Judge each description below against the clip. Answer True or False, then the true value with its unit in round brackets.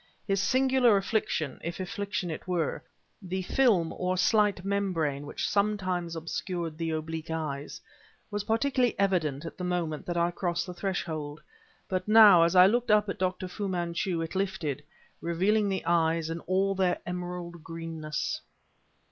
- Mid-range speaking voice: True (180 Hz)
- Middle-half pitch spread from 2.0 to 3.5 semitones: True (3.2 semitones)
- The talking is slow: False (155 wpm)